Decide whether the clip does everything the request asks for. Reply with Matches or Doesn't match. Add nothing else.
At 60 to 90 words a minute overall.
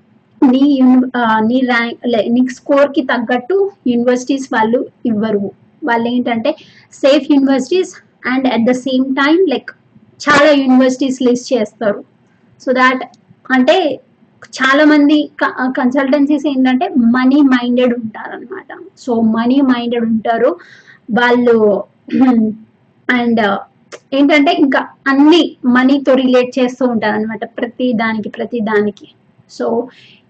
Doesn't match